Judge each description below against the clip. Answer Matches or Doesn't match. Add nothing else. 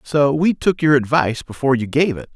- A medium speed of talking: Doesn't match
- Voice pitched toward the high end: Doesn't match